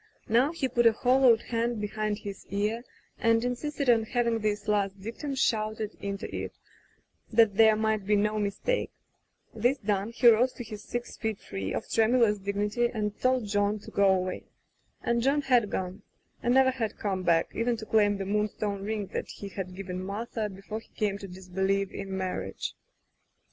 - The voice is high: Yes, high, 215 Hz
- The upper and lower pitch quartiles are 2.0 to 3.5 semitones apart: Yes, average, 2.9 semitones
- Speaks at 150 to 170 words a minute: No, average, 180 wpm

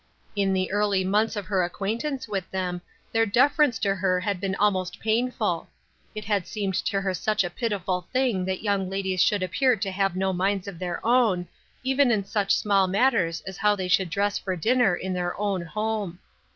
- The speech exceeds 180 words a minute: Yes, average, 195 wpm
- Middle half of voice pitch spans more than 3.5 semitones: No, narrow, 2.6 semitones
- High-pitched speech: Yes, high, 195 Hz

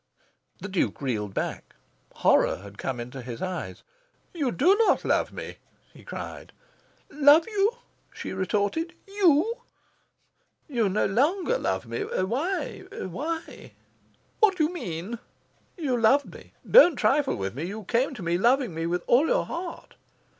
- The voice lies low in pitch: No, high, 245 Hz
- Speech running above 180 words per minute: No, average, 145 wpm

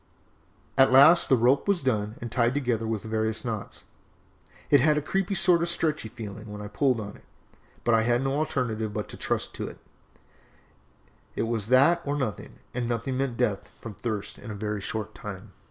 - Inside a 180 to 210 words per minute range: Yes, average, 195 wpm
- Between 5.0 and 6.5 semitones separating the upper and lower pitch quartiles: No, average, 4.0 semitones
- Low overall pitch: Yes, low, 120 Hz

